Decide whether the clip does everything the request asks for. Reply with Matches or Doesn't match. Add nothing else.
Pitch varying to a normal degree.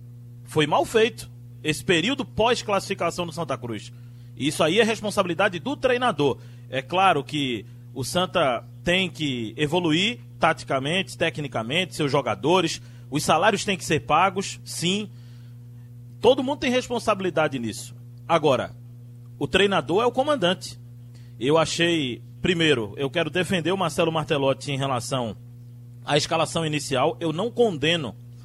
Doesn't match